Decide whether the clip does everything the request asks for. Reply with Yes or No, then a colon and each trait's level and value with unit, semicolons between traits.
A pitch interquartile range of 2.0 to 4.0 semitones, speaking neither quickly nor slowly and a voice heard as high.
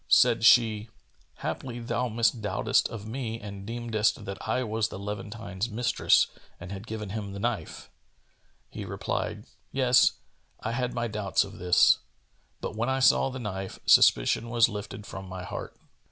No: average, 2.8 semitones; average, 155 wpm; low, 110 Hz